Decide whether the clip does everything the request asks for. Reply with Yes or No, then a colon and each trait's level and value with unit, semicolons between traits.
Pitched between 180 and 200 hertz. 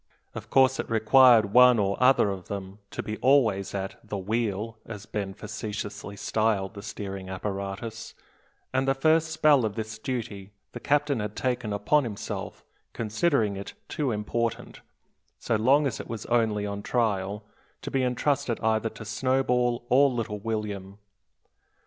No: low, 110 Hz